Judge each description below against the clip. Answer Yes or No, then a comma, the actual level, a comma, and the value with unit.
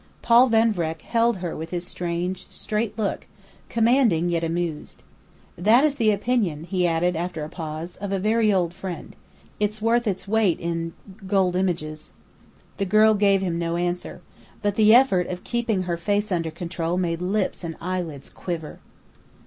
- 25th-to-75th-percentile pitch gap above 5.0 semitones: No, average, 4.0 semitones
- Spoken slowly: No, average, 170 wpm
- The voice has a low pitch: No, medium, 185 Hz